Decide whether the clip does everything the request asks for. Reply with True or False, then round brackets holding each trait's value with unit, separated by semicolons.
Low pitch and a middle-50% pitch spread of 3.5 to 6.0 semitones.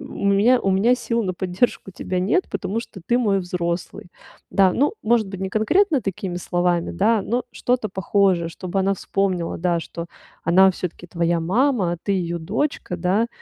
False (190 Hz; 3.9 semitones)